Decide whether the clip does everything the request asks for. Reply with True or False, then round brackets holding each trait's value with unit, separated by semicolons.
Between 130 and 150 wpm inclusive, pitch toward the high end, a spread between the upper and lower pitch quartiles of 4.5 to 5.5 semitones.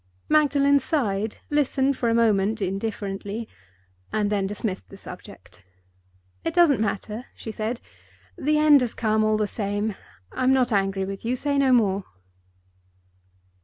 True (140 wpm; 220 Hz; 4.8 semitones)